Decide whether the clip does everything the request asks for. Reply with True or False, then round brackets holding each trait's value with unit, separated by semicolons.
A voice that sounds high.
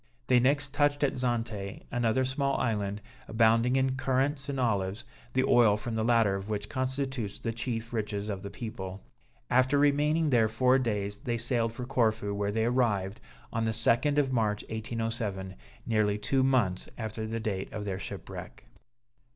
False (115 Hz)